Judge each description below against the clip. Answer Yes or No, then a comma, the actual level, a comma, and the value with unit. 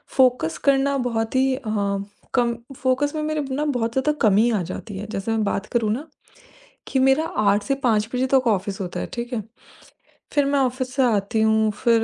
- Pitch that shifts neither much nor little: Yes, average, 3.9 semitones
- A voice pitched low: No, high, 235 Hz